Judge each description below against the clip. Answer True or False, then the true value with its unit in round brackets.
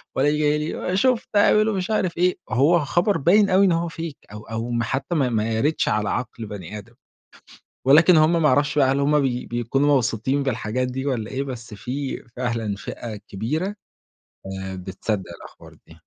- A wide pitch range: True (6.3 semitones)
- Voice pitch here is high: False (135 Hz)